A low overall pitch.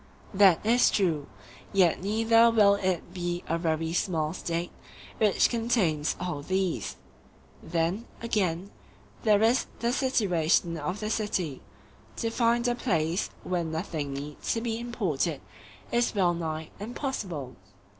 No: medium, 185 Hz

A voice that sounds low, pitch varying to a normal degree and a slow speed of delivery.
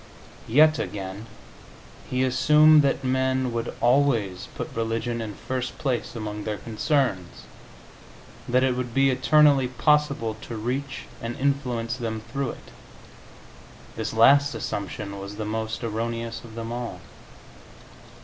Yes: low, 120 Hz; average, 3.2 semitones; slow, 130 wpm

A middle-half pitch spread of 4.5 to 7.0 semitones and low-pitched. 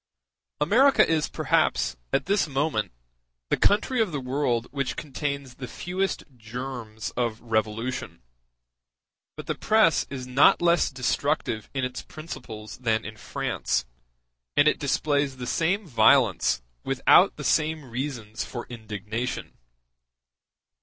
Yes: average, 4.9 semitones; low, 130 Hz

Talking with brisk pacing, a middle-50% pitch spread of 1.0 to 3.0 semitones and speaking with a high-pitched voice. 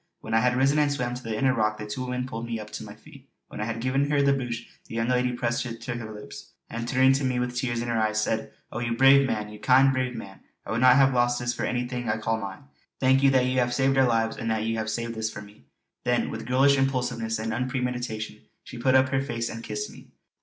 No: fast, 270 wpm; narrow, 2.5 semitones; low, 120 Hz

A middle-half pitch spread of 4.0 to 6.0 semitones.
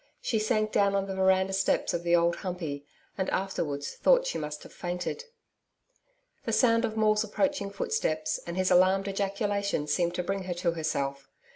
No: average, 3.1 semitones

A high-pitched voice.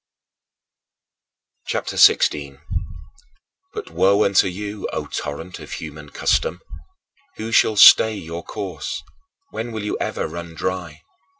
No: very low, 90 Hz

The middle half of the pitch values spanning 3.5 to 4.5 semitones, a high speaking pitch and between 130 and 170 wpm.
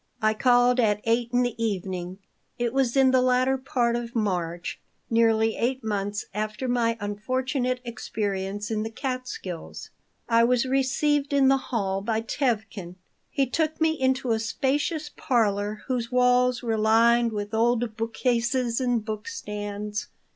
No: average, 3.0 semitones; high, 235 Hz; average, 150 wpm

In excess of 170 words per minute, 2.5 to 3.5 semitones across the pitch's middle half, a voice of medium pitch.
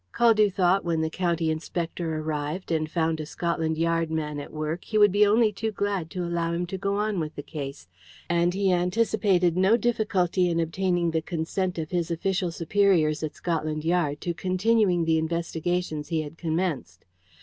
Yes: average, 180 wpm; average, 3.0 semitones; medium, 170 Hz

